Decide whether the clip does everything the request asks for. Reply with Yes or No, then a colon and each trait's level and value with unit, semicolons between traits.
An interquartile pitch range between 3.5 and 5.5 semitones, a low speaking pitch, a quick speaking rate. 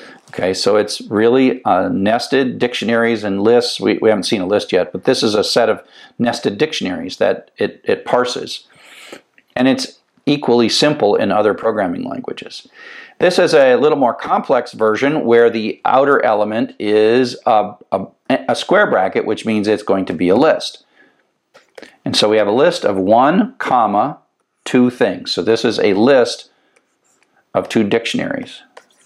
No: average, 4.4 semitones; low, 115 Hz; average, 165 wpm